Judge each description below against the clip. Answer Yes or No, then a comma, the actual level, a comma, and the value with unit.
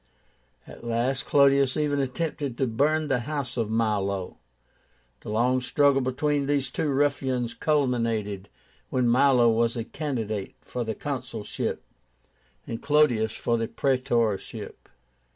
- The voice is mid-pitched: No, low, 125 Hz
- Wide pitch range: No, average, 3.6 semitones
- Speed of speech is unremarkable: No, slow, 125 wpm